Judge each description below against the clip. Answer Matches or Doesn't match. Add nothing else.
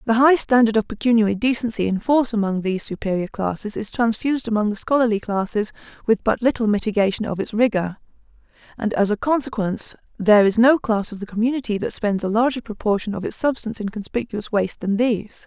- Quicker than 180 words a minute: Matches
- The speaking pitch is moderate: Doesn't match